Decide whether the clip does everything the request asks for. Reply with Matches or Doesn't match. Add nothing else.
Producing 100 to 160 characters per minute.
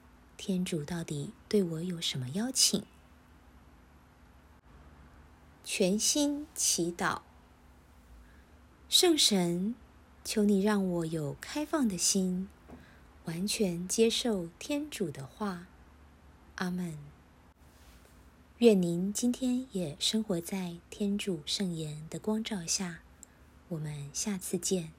Matches